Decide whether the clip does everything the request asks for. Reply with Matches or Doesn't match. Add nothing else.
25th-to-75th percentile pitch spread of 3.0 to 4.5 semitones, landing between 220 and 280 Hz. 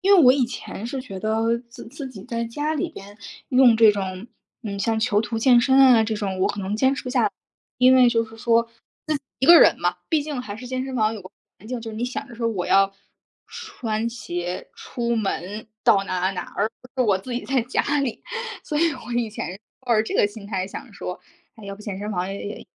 Matches